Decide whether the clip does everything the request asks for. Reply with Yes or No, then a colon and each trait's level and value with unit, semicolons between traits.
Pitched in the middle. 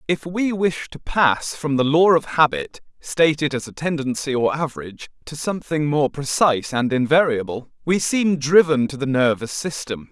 Yes: medium, 145 Hz